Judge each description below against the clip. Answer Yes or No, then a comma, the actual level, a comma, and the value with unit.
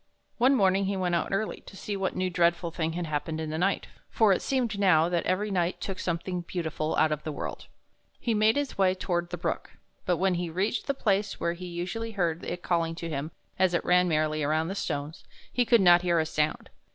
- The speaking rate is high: Yes, fast, 235 wpm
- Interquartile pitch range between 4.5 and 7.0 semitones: No, average, 2.9 semitones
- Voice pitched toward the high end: No, medium, 175 Hz